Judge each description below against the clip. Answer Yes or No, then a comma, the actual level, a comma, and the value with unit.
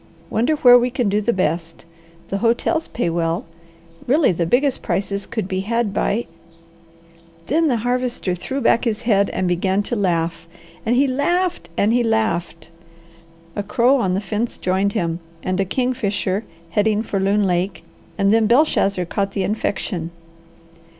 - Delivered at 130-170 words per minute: Yes, average, 165 wpm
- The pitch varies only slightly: No, average, 4.7 semitones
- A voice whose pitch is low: No, high, 205 Hz